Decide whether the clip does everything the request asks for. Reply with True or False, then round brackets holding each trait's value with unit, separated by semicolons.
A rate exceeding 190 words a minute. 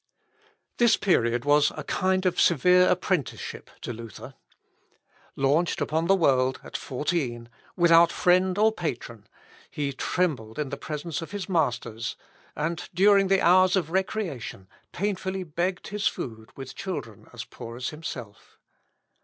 False (135 wpm)